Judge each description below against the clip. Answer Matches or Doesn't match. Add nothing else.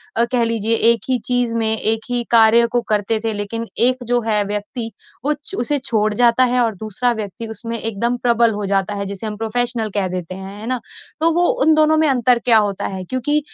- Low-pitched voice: Doesn't match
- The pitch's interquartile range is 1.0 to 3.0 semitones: Matches